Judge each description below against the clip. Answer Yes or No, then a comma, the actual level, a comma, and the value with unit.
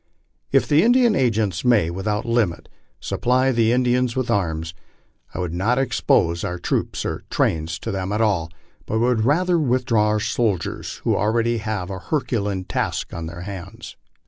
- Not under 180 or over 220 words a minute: No, average, 160 wpm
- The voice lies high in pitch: No, low, 110 Hz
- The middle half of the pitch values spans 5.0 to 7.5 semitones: Yes, average, 5.3 semitones